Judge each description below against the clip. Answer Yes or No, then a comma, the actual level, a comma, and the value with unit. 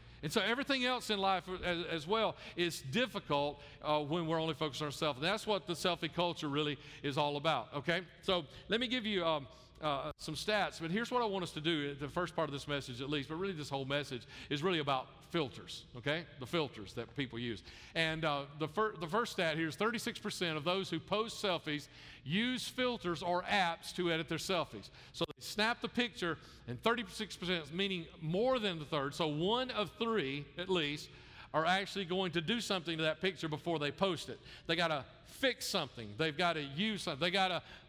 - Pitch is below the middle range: No, medium, 170 Hz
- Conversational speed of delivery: No, fast, 215 wpm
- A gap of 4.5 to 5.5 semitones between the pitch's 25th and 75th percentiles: Yes, average, 4.9 semitones